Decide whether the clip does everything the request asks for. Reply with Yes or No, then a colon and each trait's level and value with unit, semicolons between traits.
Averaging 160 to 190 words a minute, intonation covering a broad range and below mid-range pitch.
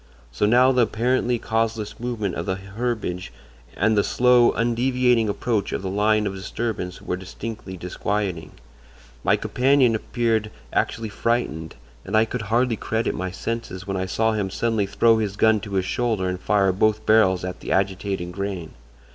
No: average, 165 wpm; average, 3.4 semitones; low, 105 Hz